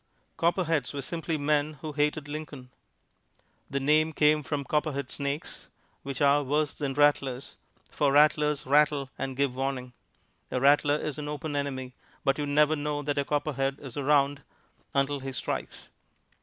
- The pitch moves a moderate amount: No, narrow, 1.6 semitones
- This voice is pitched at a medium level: Yes, medium, 145 Hz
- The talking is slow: No, average, 155 wpm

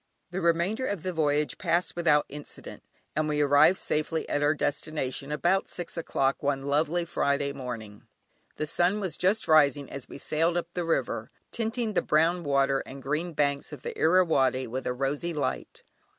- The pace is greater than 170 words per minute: Yes, average, 180 wpm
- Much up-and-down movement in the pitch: No, average, 3.5 semitones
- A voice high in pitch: No, medium, 150 Hz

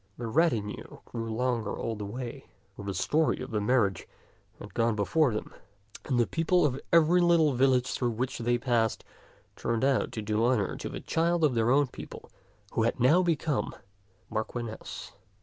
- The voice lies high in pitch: No, low, 120 Hz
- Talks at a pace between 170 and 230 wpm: Yes, average, 185 wpm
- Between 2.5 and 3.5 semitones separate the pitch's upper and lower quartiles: No, average, 4.6 semitones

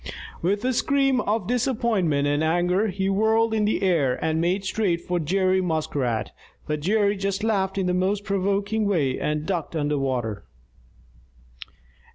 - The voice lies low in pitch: No, high, 190 Hz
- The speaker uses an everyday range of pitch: Yes, average, 4.7 semitones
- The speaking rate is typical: Yes, average, 155 wpm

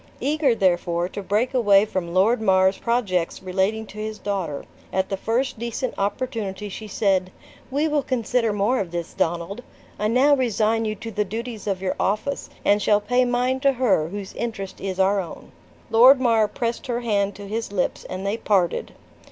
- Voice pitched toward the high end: Yes, high, 210 Hz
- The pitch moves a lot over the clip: No, average, 3.7 semitones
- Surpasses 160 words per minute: Yes, average, 185 wpm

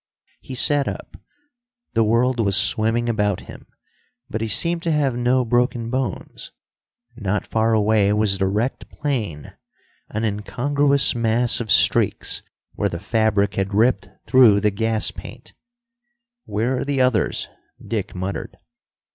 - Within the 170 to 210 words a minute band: No, average, 140 wpm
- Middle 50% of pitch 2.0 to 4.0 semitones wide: Yes, average, 3.5 semitones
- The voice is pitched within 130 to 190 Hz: No, low, 115 Hz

